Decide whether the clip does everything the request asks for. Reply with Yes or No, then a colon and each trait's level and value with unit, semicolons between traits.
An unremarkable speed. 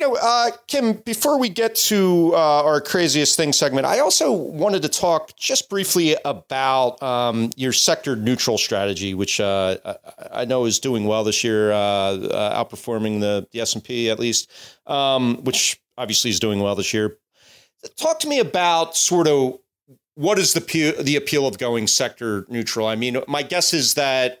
Yes: average, 185 wpm